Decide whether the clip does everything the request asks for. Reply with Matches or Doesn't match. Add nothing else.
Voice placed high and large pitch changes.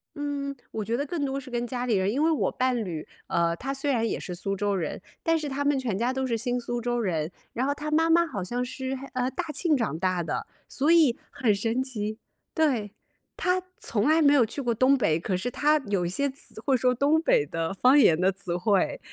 Matches